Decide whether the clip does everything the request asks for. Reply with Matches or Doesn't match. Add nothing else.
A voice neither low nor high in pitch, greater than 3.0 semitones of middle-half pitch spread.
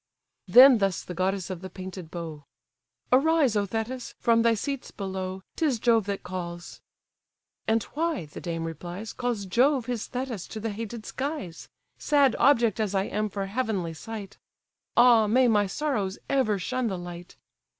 Doesn't match